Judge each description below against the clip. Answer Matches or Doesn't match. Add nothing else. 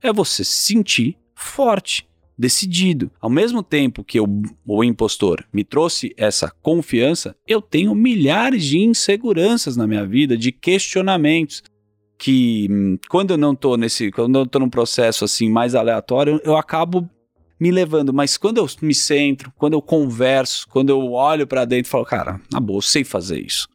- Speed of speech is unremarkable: Matches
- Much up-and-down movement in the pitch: Matches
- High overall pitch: Doesn't match